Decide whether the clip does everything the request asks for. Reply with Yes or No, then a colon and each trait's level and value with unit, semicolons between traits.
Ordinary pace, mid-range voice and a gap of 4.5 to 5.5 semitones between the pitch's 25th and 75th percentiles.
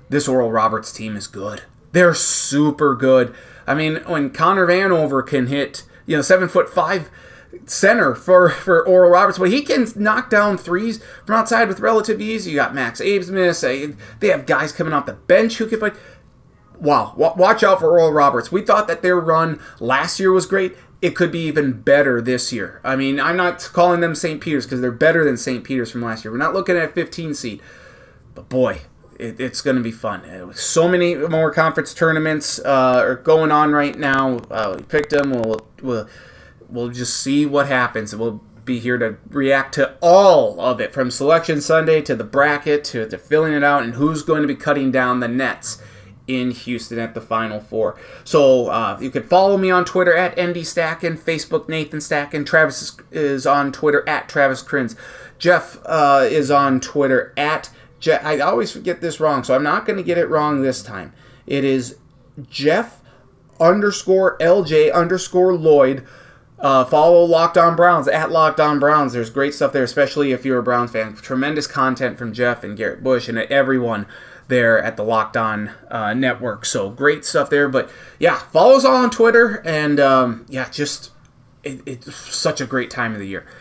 Yes: average, 195 wpm; medium, 145 Hz; average, 4.9 semitones